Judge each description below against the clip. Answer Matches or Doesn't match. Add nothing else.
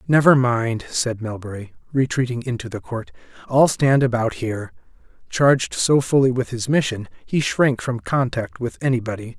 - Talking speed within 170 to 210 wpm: Doesn't match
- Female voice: Doesn't match